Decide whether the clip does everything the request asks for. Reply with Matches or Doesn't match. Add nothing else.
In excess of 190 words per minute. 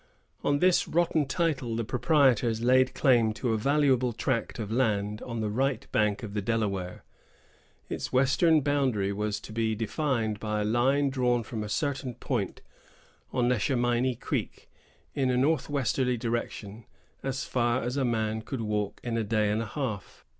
Doesn't match